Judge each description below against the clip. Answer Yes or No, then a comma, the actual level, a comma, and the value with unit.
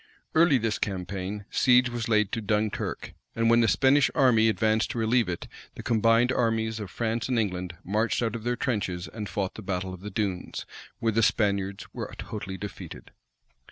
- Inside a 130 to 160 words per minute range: No, average, 185 wpm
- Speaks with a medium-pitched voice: No, low, 110 Hz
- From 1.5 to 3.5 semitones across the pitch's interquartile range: Yes, average, 2.9 semitones